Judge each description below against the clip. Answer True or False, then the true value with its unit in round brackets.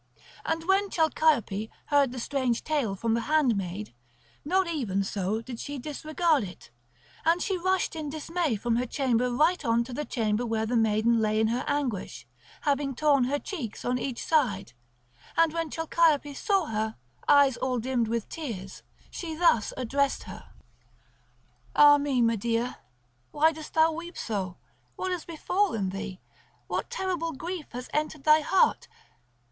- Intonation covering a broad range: True (5.7 semitones)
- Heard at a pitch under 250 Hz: False (275 Hz)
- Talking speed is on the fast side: False (155 wpm)